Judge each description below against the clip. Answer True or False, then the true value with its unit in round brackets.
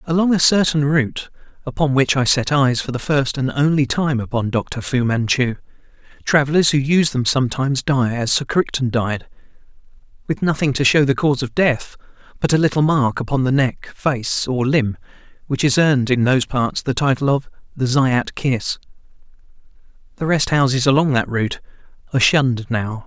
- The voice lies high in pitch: False (135 Hz)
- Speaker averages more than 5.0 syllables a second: True (5.3 syllables/s)